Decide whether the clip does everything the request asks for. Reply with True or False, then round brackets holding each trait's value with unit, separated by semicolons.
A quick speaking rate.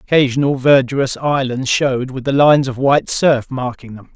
False (175 wpm)